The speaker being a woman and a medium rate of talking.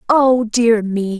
Yes: female; average, 150 wpm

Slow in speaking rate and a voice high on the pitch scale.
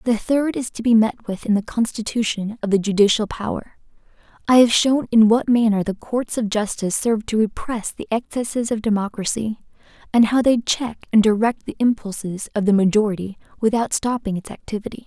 No: average, 185 wpm; high, 220 Hz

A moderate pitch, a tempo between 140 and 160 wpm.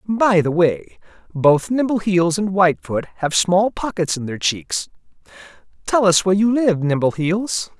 Yes: medium, 180 Hz; average, 145 wpm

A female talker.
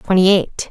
Yes: female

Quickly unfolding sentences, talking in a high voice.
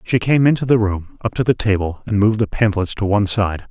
No: fast, 260 wpm; low, 105 Hz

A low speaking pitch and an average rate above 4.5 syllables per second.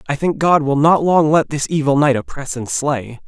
No: medium, 145 Hz; 5.0 syllables/s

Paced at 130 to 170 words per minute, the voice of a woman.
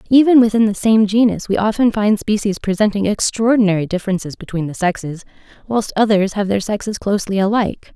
Yes: average, 165 wpm; female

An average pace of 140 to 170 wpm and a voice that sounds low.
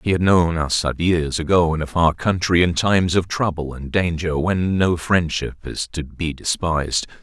No: average, 190 wpm; very low, 85 Hz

